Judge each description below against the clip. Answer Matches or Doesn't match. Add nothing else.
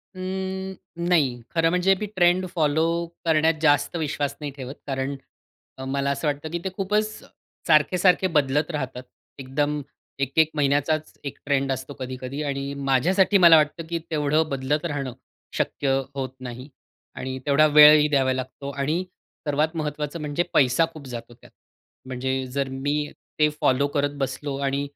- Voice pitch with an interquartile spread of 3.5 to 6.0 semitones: Doesn't match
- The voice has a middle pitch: Matches